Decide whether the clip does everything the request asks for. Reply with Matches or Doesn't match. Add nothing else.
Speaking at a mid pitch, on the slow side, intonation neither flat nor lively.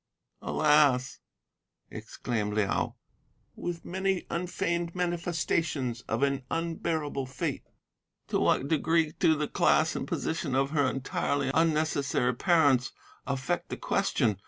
Matches